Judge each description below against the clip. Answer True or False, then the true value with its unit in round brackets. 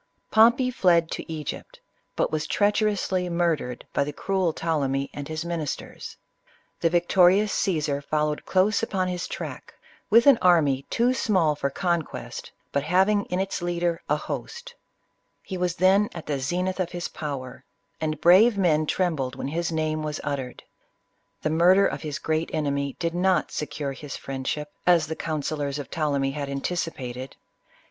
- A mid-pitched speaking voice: True (165 Hz)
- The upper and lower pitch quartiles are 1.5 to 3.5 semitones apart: False (3.9 semitones)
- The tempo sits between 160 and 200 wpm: True (170 wpm)